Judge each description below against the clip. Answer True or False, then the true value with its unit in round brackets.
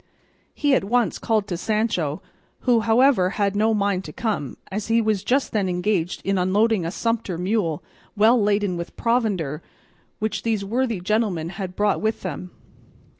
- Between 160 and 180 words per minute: True (165 wpm)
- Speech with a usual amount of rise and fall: True (3.6 semitones)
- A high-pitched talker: True (205 Hz)